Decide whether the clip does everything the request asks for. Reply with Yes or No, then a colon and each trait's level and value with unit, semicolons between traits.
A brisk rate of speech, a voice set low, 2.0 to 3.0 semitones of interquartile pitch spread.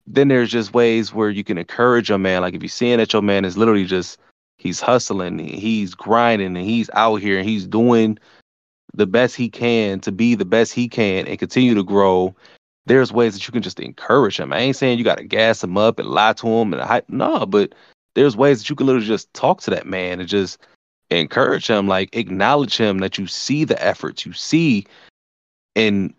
No: fast, 220 wpm; low, 110 Hz; average, 3.6 semitones